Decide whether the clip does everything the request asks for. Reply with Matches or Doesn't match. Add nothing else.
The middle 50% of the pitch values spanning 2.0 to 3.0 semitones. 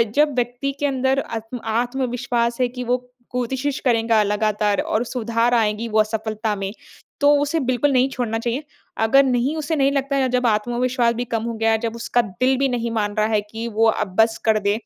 Matches